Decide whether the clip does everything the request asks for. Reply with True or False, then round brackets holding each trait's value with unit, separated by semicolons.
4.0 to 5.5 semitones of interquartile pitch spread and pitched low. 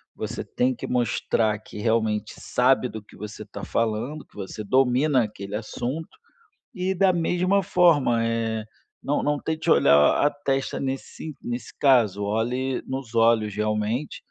True (5.0 semitones; 120 Hz)